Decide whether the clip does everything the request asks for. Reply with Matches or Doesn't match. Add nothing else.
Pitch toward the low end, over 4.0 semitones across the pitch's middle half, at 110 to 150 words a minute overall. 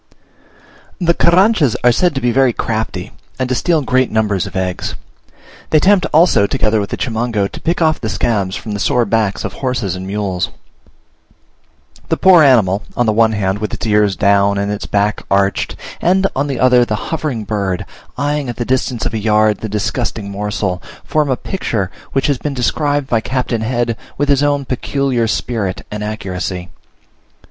Doesn't match